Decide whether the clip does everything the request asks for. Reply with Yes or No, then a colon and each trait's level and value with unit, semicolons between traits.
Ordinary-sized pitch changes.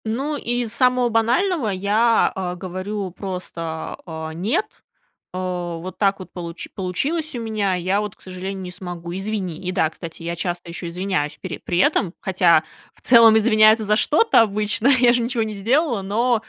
Yes: average, 4.2 semitones